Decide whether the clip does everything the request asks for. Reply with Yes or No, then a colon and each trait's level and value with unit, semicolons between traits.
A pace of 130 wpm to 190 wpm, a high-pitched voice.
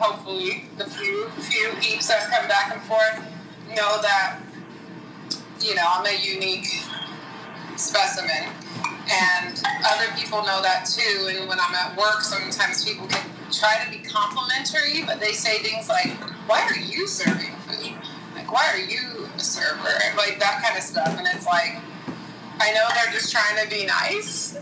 Yes: average, 170 wpm; high, 210 Hz